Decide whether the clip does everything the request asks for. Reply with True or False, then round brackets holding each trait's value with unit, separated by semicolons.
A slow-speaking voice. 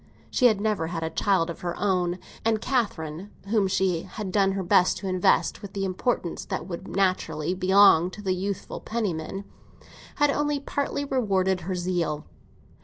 False (170 wpm)